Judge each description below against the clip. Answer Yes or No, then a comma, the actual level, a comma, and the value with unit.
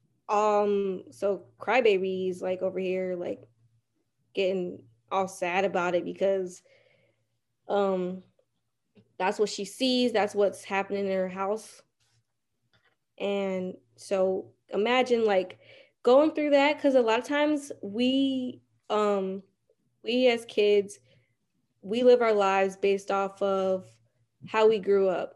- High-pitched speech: Yes, high, 195 Hz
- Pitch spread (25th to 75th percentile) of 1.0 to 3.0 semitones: Yes, average, 2.7 semitones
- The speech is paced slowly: Yes, slow, 125 wpm